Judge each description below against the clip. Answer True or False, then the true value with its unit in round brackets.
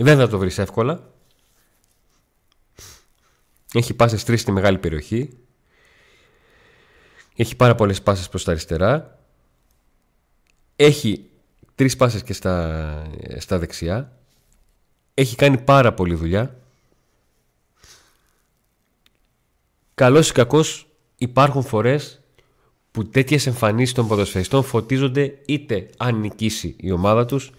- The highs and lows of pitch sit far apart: True (6.1 semitones)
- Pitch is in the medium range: False (115 Hz)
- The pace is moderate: True (130 wpm)